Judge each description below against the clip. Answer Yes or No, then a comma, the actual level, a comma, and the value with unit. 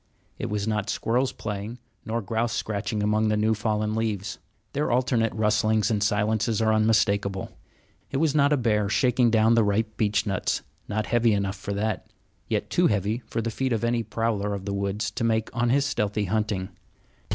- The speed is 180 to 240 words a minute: Yes, average, 185 wpm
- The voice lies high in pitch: No, low, 110 Hz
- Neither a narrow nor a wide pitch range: No, narrow, 1.9 semitones